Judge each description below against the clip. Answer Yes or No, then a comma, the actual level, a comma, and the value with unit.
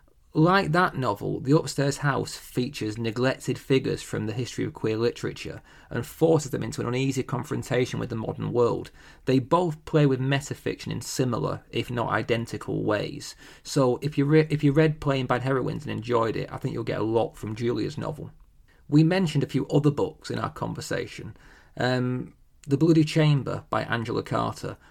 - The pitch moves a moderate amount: Yes, average, 3.8 semitones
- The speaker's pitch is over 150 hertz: No, low, 135 Hz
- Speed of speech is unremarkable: Yes, average, 180 wpm